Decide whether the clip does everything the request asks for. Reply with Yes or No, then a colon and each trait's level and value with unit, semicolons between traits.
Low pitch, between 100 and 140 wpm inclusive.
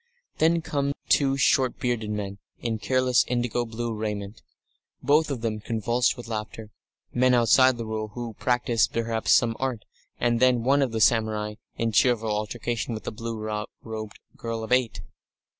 No: low, 115 Hz; average, 160 wpm